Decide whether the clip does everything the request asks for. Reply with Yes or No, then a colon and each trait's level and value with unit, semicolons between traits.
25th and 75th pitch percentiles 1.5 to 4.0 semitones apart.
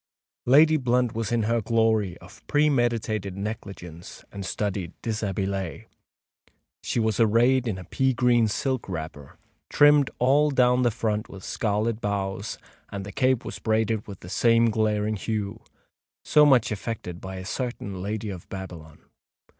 Yes: average, 3.7 semitones